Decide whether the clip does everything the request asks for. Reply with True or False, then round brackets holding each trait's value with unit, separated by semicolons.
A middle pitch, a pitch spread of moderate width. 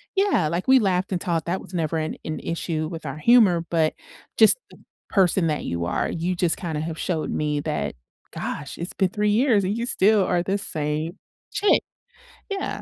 True (175 Hz; 4.2 semitones)